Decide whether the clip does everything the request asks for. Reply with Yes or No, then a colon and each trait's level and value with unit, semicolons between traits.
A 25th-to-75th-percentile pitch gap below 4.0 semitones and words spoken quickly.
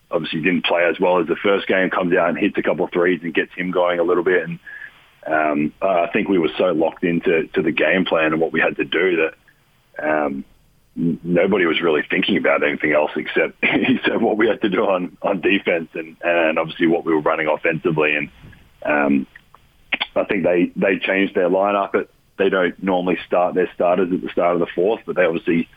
Yes: average, 3.0 semitones; fast, 225 wpm